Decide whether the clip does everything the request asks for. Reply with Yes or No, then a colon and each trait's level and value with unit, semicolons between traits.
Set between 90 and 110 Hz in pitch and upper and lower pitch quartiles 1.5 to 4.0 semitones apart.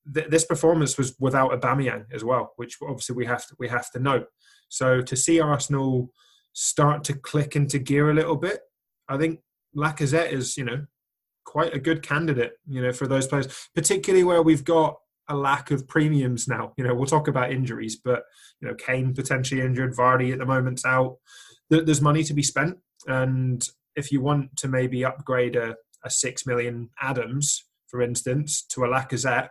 No: low, 135 Hz; average, 3.0 semitones